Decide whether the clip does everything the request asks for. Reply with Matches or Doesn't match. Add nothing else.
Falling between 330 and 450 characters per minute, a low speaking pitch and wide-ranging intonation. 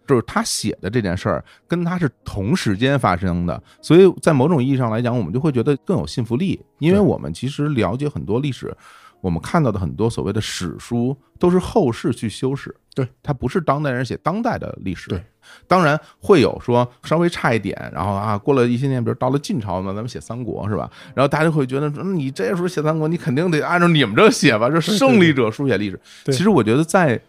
Matches